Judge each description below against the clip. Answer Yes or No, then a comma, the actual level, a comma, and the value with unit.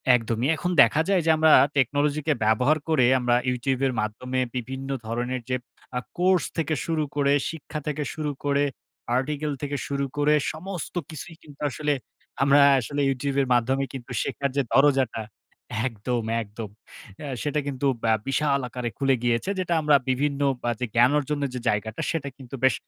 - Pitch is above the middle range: No, medium, 140 Hz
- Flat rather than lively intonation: No, average, 3.2 semitones